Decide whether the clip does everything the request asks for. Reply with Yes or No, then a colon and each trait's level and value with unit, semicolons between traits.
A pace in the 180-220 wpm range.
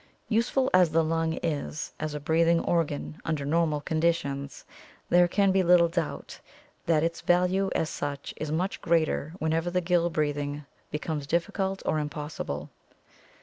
No: average, 145 wpm